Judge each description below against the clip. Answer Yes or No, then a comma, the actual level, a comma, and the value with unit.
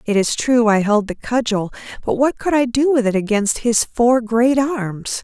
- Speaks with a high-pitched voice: Yes, high, 235 Hz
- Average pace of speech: No, fast, 220 wpm